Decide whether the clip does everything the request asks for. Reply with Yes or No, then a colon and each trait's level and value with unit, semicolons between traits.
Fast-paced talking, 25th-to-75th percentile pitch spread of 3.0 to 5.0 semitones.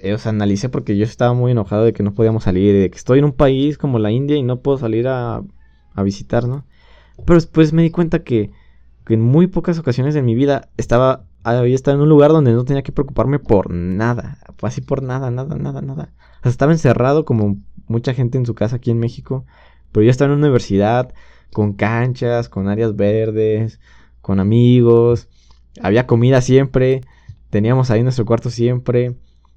Yes: fast, 195 wpm; average, 3.9 semitones